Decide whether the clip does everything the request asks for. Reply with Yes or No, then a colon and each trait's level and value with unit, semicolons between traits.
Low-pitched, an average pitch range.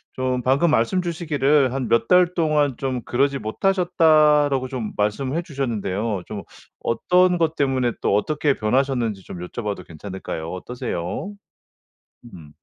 No: low, 130 Hz; wide, 6.0 semitones